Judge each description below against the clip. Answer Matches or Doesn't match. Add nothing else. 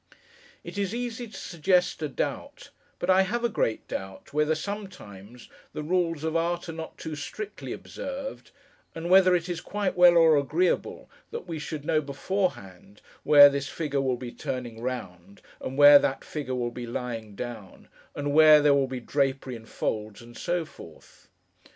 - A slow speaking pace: Doesn't match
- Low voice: Doesn't match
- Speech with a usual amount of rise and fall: Doesn't match